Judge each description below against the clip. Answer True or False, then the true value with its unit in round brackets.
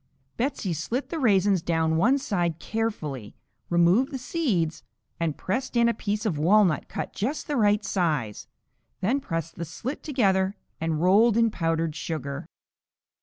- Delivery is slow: False (150 wpm)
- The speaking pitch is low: False (190 Hz)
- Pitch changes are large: True (6.0 semitones)